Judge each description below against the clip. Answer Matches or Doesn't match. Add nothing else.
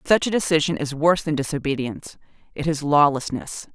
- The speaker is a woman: Matches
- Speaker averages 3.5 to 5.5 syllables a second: Doesn't match